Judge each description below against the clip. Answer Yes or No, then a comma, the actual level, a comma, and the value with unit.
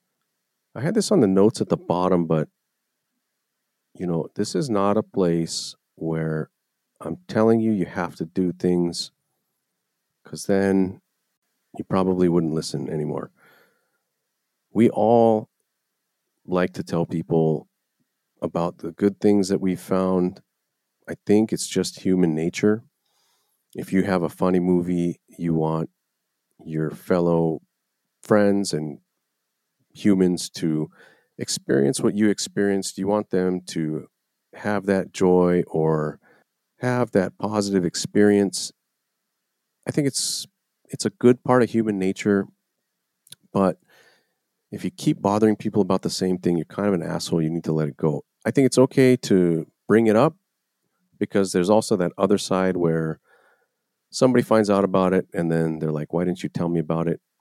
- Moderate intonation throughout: Yes, average, 4.0 semitones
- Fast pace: No, average, 150 wpm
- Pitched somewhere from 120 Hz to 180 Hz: No, very low, 95 Hz